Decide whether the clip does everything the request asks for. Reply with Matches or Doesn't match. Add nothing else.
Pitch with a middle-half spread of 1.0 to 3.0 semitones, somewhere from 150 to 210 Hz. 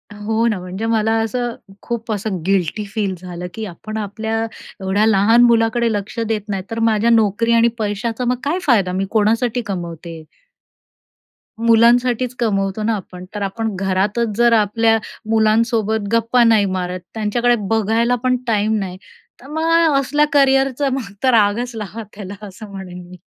Doesn't match